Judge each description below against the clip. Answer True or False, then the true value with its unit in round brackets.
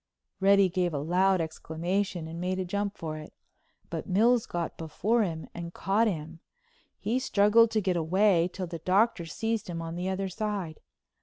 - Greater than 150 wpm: True (175 wpm)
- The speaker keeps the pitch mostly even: False (3.5 semitones)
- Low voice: False (185 Hz)